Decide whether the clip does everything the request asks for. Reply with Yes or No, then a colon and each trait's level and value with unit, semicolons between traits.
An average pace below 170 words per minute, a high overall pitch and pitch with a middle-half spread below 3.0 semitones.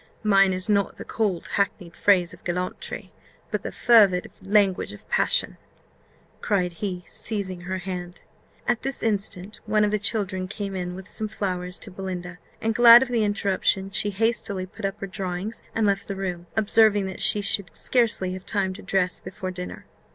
No: average, 180 wpm; high, 195 Hz; narrow, 2.5 semitones